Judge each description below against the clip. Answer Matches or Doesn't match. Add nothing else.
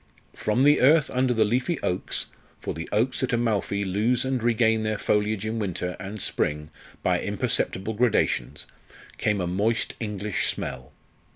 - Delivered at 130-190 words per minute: Matches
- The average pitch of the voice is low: Matches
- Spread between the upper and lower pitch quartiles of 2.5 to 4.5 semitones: Matches